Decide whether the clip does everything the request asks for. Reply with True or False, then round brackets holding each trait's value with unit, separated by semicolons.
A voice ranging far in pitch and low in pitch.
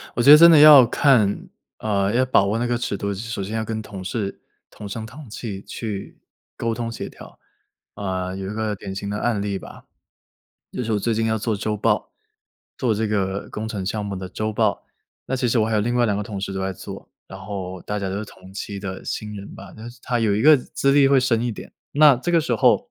False (3.3 semitones; 110 Hz)